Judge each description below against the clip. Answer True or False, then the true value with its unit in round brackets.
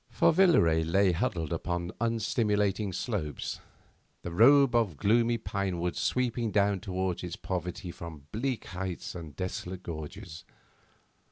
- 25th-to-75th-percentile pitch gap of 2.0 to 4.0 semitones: False (4.6 semitones)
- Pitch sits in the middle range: False (95 Hz)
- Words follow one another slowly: True (125 wpm)